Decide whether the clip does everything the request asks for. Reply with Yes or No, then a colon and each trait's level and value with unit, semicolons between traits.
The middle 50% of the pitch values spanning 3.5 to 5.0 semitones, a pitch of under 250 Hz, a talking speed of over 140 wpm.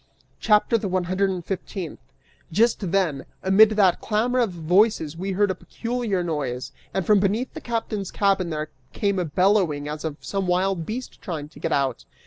Yes: average, 4.0 semitones; high, 190 Hz; average, 180 wpm